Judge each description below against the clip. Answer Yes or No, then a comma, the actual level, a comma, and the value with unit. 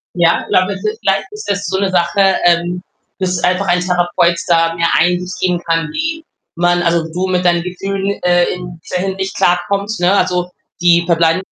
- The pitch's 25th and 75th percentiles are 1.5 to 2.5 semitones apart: Yes, narrow, 1.8 semitones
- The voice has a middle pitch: Yes, medium, 180 Hz